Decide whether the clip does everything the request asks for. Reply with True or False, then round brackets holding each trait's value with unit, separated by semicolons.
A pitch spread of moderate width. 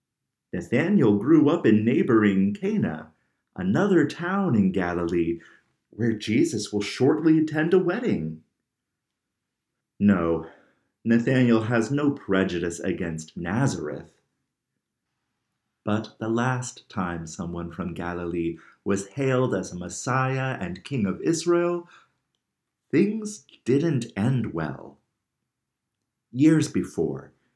False (8.4 semitones)